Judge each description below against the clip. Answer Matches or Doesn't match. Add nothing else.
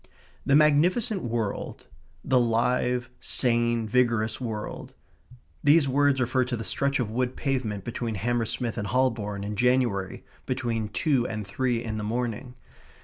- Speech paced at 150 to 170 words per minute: Doesn't match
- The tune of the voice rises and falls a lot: Doesn't match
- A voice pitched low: Matches